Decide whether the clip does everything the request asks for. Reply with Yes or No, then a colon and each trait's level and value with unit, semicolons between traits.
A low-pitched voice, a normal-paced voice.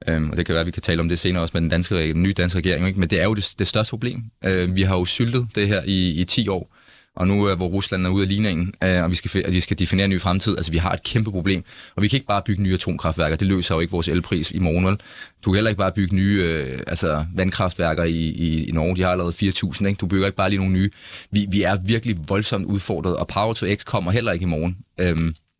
No: very low, 95 Hz; fast, 270 wpm